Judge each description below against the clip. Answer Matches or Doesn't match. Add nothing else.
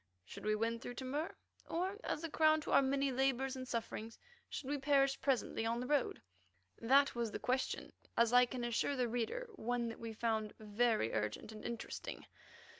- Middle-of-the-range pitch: Doesn't match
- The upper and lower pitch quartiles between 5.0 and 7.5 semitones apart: Doesn't match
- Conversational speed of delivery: Matches